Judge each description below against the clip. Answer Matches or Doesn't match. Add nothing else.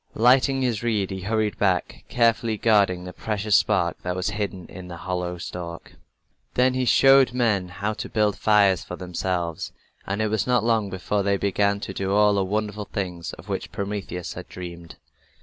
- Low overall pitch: Matches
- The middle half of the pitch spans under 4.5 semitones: Matches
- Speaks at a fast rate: Doesn't match